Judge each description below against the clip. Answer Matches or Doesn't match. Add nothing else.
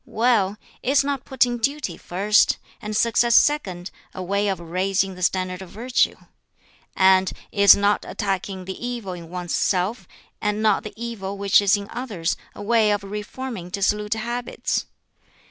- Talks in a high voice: Matches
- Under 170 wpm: Matches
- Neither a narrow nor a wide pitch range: Matches